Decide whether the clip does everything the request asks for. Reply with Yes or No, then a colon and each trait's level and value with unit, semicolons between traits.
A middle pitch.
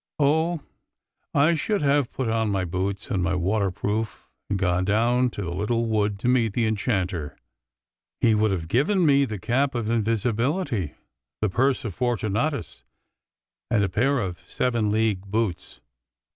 No: low, 110 Hz